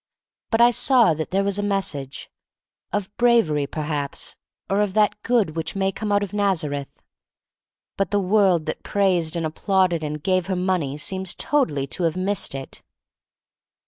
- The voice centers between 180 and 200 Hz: Yes, medium, 185 Hz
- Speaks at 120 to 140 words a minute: No, average, 175 wpm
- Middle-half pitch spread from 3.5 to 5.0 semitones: Yes, average, 4.5 semitones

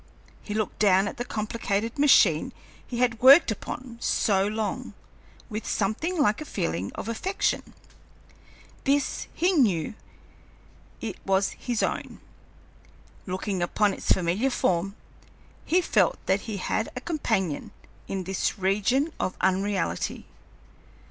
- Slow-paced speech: Yes, slow, 125 wpm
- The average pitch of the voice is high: Yes, high, 210 Hz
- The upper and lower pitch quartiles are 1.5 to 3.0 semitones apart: No, average, 4.5 semitones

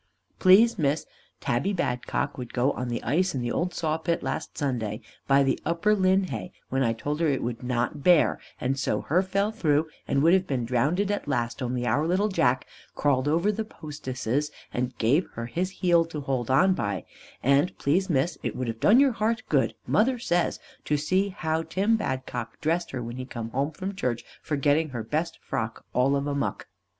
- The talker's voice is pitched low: No, medium, 145 Hz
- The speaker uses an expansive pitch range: Yes, wide, 6.3 semitones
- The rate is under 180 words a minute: No, average, 200 wpm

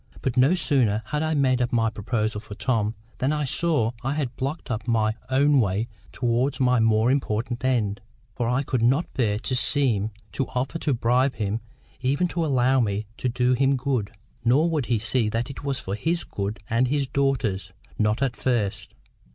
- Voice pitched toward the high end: No, low, 125 Hz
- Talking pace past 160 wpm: Yes, average, 190 wpm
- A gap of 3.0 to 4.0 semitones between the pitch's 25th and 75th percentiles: Yes, average, 3.7 semitones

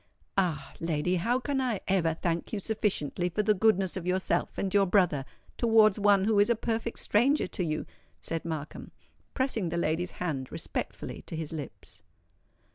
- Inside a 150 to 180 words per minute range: Yes, average, 170 wpm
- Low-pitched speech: No, medium, 185 Hz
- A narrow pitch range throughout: No, average, 4.6 semitones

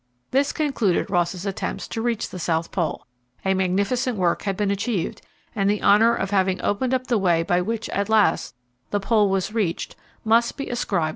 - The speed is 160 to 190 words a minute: No, average, 200 wpm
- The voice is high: Yes, high, 200 Hz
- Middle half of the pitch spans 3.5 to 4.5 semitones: Yes, average, 3.8 semitones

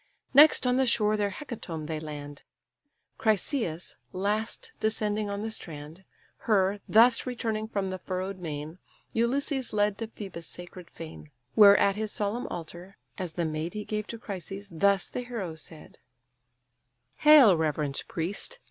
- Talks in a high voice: Yes, high, 200 Hz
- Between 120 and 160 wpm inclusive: Yes, average, 150 wpm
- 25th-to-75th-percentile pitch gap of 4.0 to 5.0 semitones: Yes, average, 4.6 semitones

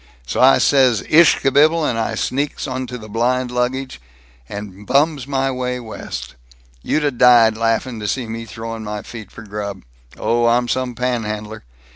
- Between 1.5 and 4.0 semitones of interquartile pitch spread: Yes, average, 2.9 semitones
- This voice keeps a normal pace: Yes, average, 165 wpm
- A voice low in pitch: Yes, low, 120 Hz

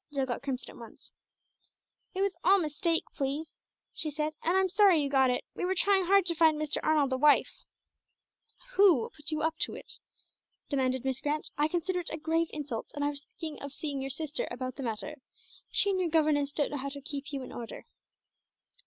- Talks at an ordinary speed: No, fast, 215 wpm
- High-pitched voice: Yes, very high, 300 Hz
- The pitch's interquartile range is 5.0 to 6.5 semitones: No, average, 3.2 semitones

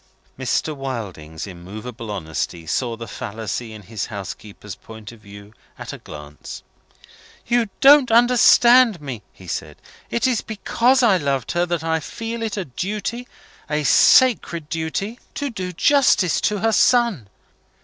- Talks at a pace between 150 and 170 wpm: No, average, 140 wpm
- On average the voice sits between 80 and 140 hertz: No, medium, 150 Hz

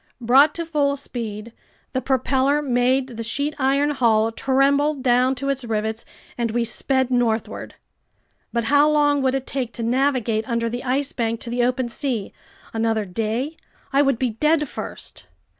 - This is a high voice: Yes, very high, 255 Hz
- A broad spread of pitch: No, average, 3.2 semitones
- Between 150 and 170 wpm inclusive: Yes, average, 165 wpm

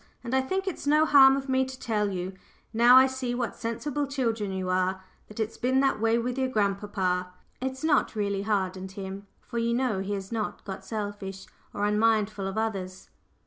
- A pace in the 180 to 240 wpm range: Yes, average, 195 wpm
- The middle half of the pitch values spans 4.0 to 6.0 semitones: Yes, average, 4.9 semitones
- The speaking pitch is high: Yes, high, 220 Hz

